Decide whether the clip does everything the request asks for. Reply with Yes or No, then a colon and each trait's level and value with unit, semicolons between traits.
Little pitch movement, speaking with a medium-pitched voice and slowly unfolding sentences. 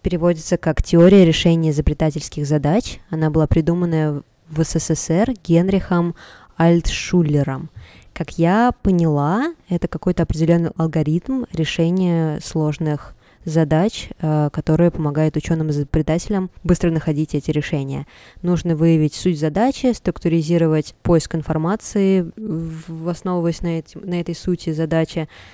Yes: narrow, 2.0 semitones; medium, 165 Hz; slow, 105 wpm